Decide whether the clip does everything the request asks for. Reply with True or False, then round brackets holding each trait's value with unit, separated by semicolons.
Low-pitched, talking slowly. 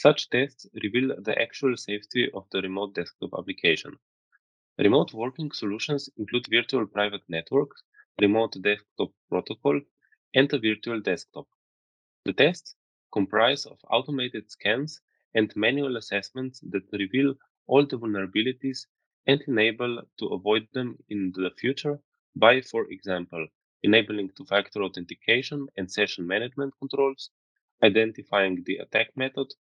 True (115 Hz; 125 wpm)